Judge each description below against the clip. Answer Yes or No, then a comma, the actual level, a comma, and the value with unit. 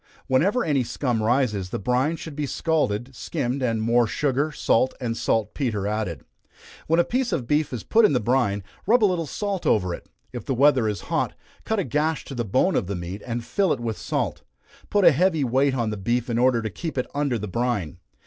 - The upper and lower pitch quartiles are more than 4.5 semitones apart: Yes, average, 5.2 semitones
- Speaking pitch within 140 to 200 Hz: No, low, 125 Hz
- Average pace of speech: No, fast, 225 wpm